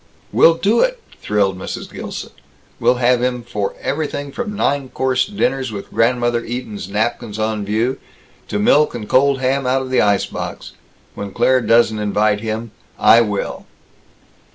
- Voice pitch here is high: No, low, 120 Hz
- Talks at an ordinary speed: Yes, average, 155 wpm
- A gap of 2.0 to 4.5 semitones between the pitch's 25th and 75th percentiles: Yes, average, 3.8 semitones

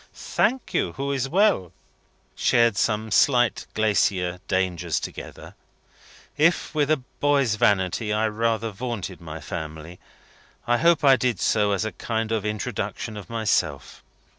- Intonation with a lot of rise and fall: No, average, 4.8 semitones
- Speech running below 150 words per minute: Yes, average, 140 wpm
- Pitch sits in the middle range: No, low, 110 Hz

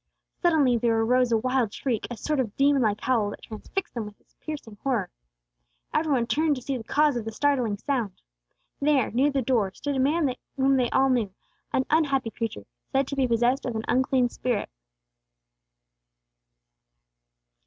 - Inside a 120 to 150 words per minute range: No, average, 175 wpm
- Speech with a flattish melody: No, average, 3.5 semitones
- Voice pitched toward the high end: Yes, very high, 255 Hz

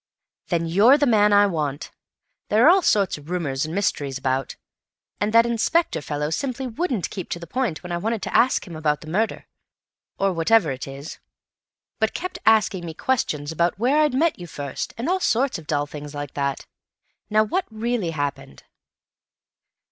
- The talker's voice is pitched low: No, medium, 185 Hz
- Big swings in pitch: Yes, wide, 7.6 semitones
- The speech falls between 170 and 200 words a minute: Yes, average, 185 wpm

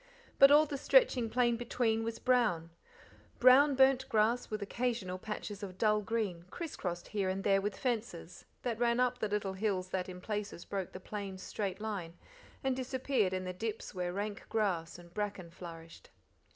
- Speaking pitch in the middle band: No, high, 210 Hz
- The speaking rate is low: No, average, 180 wpm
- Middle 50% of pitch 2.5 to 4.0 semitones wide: No, average, 4.5 semitones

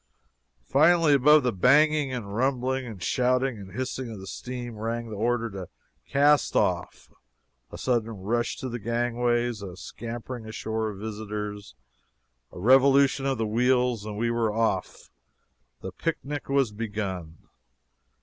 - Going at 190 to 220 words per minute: No, average, 140 wpm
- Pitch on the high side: No, low, 120 Hz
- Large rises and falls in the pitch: No, average, 3.5 semitones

